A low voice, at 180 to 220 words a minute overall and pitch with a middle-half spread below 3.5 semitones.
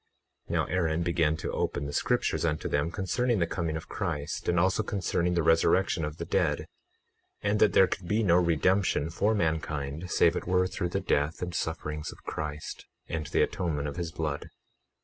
Yes: very low, 85 Hz; average, 190 wpm; average, 3.0 semitones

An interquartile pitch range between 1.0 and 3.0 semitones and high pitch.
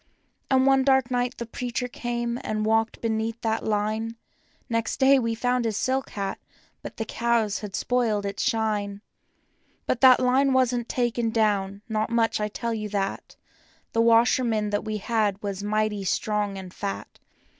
Yes: narrow, 2.4 semitones; high, 225 Hz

